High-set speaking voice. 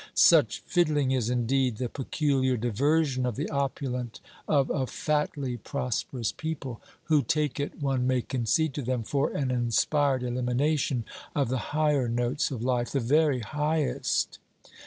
No: low, 130 Hz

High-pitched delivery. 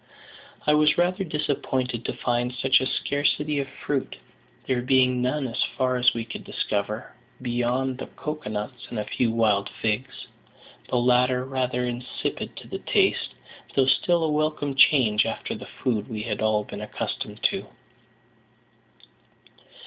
No: low, 125 Hz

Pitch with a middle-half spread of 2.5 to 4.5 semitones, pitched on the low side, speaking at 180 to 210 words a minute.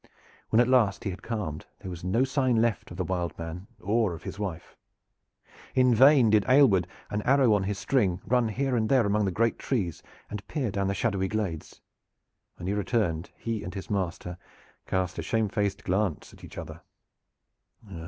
Yes: average, 4.0 semitones; low, 105 Hz; average, 185 wpm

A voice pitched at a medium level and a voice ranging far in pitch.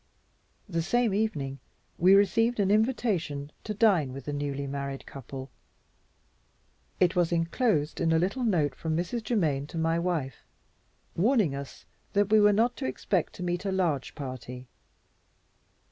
Yes: medium, 170 Hz; wide, 6.6 semitones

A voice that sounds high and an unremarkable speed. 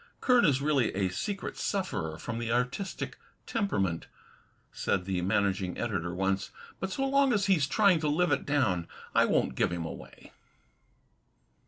No: low, 125 Hz; average, 155 wpm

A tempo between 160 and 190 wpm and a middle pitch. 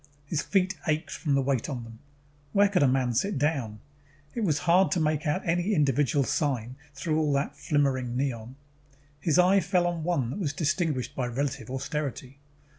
Yes: average, 185 wpm; medium, 145 Hz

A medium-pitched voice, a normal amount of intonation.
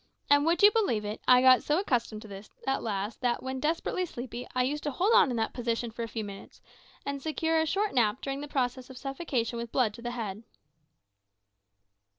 No: very high, 255 Hz; average, 4.3 semitones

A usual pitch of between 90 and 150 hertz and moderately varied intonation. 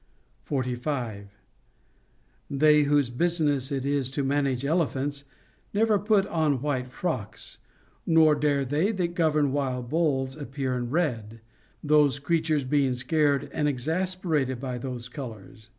Yes: medium, 140 Hz; average, 3.3 semitones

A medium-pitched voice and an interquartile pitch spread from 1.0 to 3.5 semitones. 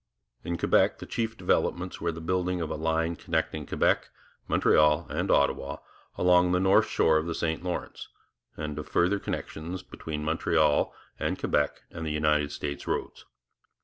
No: very low, 80 Hz; average, 2.7 semitones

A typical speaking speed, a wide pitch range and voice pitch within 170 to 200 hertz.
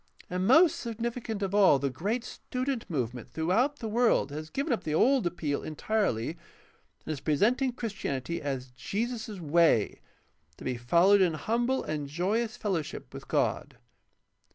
Yes: average, 150 wpm; wide, 7.5 semitones; high, 190 Hz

